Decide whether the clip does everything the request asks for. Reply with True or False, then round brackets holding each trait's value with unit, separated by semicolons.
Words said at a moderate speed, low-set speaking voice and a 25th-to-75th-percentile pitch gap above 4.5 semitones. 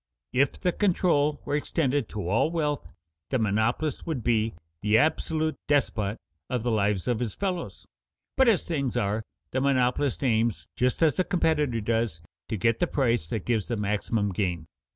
True (170 wpm; 125 Hz; 5.5 semitones)